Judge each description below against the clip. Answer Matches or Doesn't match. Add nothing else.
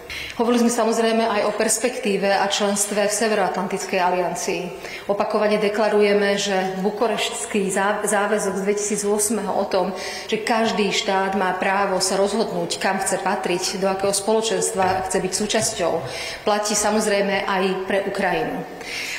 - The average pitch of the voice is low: Doesn't match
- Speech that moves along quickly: Doesn't match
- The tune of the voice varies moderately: Doesn't match